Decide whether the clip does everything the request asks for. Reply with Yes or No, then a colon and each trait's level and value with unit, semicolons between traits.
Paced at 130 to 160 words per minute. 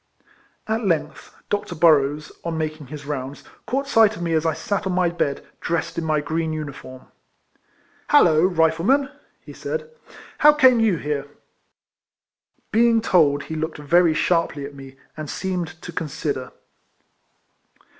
Yes: average, 150 wpm